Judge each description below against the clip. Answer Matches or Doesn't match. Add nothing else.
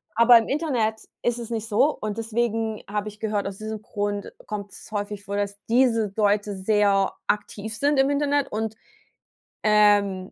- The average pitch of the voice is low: Doesn't match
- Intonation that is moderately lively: Doesn't match